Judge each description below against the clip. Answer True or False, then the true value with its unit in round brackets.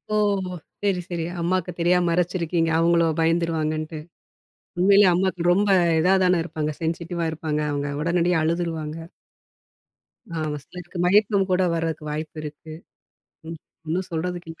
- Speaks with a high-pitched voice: False (170 Hz)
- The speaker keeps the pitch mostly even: True (2.1 semitones)